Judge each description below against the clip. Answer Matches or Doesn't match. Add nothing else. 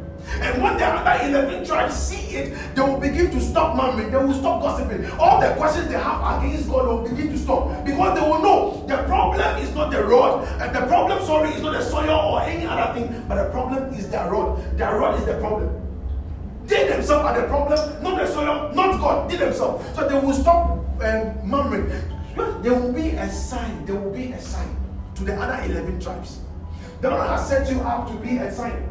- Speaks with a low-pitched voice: Doesn't match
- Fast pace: Matches